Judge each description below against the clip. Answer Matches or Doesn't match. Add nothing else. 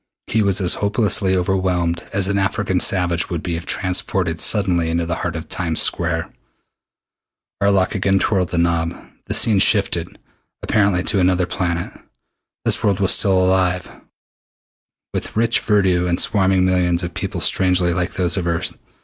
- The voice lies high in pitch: Doesn't match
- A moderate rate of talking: Matches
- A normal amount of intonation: Doesn't match